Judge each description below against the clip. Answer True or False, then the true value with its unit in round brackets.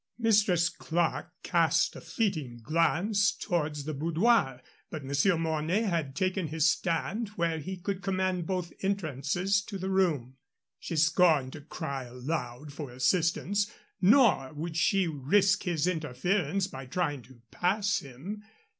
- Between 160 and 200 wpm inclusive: False (135 wpm)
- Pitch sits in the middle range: True (165 Hz)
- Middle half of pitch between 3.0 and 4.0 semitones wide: False (4.7 semitones)